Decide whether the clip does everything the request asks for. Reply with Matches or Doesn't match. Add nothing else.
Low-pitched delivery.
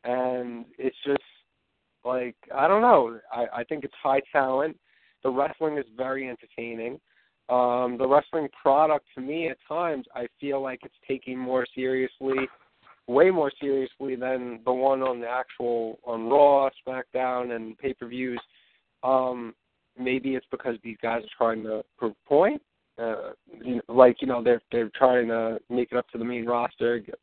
Matches